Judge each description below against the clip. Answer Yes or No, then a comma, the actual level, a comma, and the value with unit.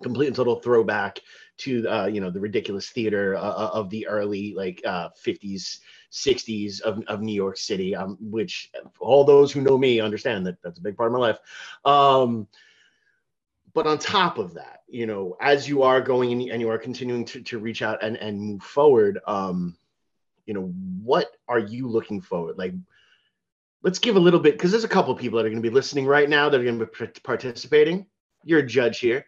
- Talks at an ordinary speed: No, fast, 210 wpm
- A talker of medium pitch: No, low, 115 Hz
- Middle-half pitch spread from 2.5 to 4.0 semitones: No, average, 4.9 semitones